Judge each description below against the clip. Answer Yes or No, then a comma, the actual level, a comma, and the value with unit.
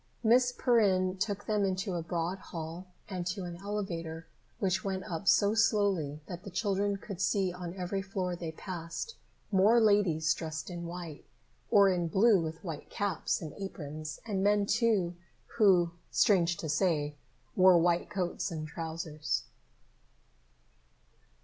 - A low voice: No, medium, 185 Hz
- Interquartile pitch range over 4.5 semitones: No, average, 3.2 semitones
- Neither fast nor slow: Yes, average, 145 wpm